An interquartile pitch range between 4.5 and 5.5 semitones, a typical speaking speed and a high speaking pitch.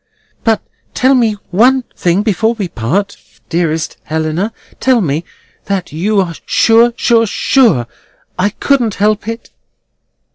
No: average, 4.9 semitones; slow, 120 wpm; high, 205 Hz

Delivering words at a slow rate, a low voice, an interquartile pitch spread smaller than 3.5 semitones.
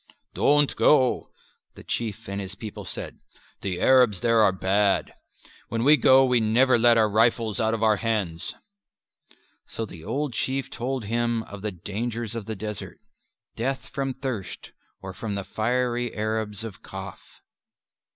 No: average, 155 wpm; low, 115 Hz; average, 2.9 semitones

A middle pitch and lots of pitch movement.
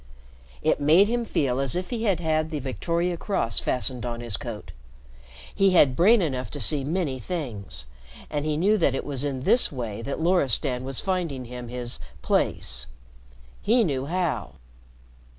Yes: medium, 145 Hz; wide, 5.9 semitones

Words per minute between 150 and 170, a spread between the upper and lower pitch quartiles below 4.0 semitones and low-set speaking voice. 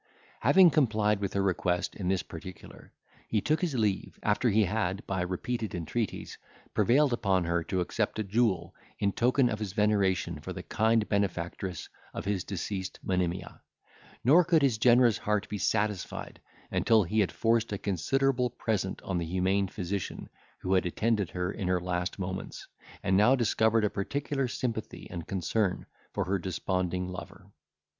Yes: average, 165 wpm; average, 3.5 semitones; low, 100 Hz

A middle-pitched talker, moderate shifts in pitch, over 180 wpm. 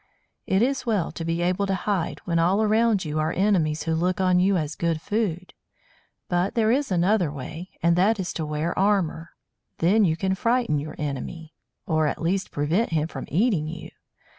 Yes: medium, 175 Hz; average, 3.9 semitones; average, 190 wpm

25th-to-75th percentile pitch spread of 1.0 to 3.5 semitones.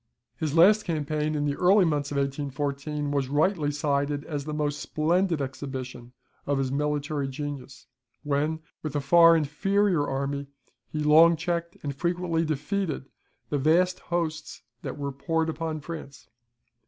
Yes: narrow, 2.6 semitones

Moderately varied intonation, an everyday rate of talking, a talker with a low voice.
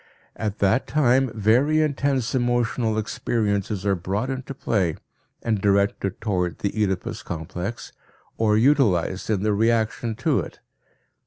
No: average, 3.6 semitones; slow, 130 wpm; low, 110 Hz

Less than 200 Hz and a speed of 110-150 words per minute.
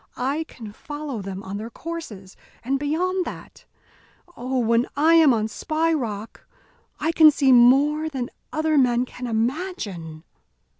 No: very high, 260 Hz; average, 145 wpm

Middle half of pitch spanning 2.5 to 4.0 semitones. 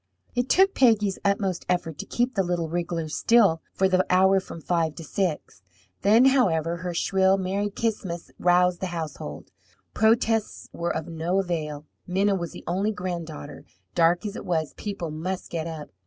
Yes: average, 3.2 semitones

